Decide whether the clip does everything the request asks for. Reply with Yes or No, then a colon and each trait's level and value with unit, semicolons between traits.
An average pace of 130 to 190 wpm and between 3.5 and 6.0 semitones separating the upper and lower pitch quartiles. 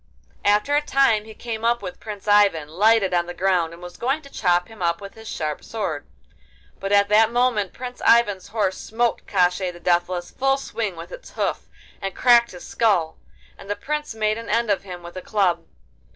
No: fast, 205 wpm; average, 4.4 semitones